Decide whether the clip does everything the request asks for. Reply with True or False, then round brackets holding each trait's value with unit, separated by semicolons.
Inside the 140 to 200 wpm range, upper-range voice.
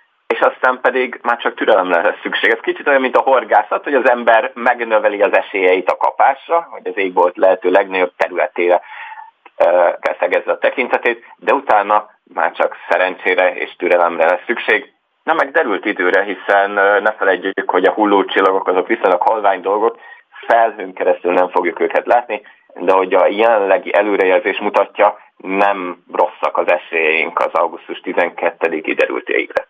True (150 wpm; 375 Hz)